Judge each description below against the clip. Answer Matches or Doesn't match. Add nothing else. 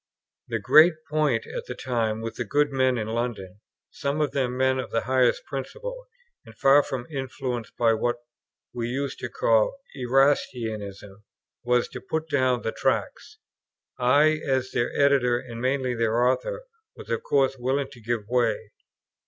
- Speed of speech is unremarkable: Matches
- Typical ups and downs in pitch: Matches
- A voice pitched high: Doesn't match